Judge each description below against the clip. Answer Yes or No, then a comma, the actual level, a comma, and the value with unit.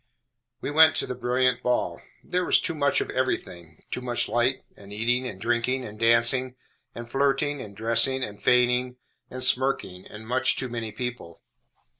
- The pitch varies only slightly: Yes, narrow, 2.1 semitones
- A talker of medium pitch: No, low, 125 Hz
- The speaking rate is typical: Yes, average, 170 wpm